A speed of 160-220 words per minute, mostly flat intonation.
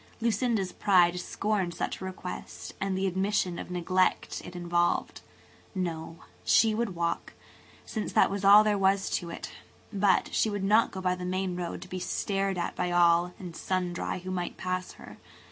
Yes: average, 180 wpm; narrow, 1.9 semitones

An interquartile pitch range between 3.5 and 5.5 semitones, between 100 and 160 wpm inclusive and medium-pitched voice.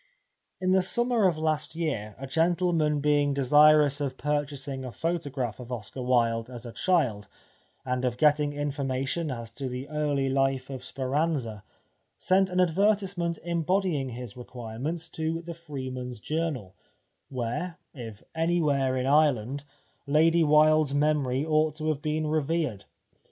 Yes: average, 4.0 semitones; average, 140 wpm; medium, 145 Hz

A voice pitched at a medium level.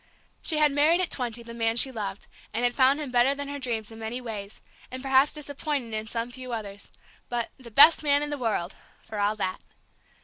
No: high, 245 Hz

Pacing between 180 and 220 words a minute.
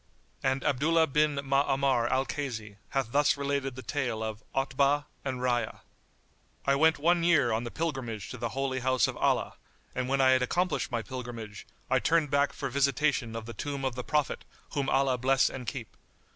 Yes: average, 185 wpm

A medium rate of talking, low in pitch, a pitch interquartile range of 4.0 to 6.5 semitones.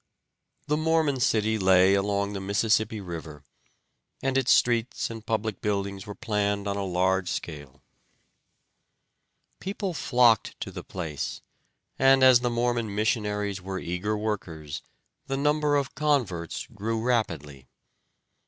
No: slow, 125 wpm; low, 105 Hz; average, 4.4 semitones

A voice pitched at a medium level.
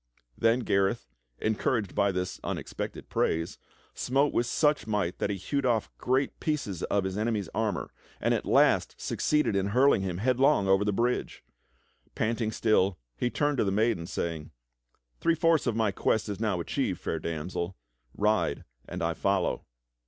No: low, 110 Hz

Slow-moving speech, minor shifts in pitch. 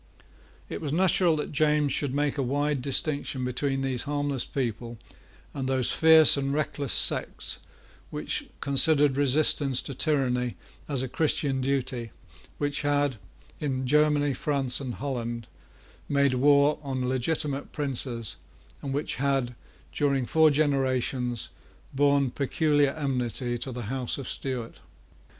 Yes: slow, 130 wpm; narrow, 2.2 semitones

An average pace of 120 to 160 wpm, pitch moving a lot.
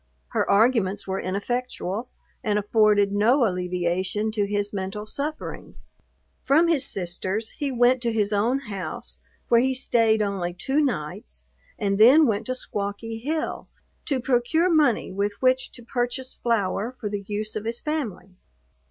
No: average, 150 wpm; average, 4.2 semitones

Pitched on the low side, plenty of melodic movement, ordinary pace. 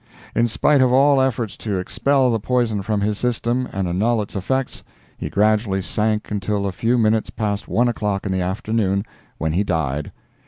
No: low, 105 Hz; average, 3.5 semitones; average, 185 wpm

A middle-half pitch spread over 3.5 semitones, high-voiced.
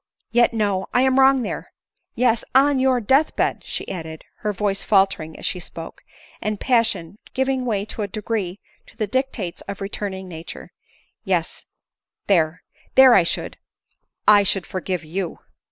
Yes: average, 4.8 semitones; high, 205 Hz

